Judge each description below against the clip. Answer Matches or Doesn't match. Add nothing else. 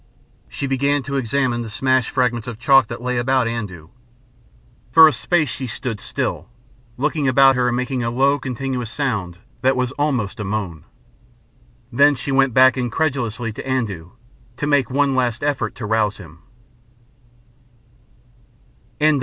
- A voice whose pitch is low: Matches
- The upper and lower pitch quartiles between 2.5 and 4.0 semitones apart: Matches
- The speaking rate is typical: Matches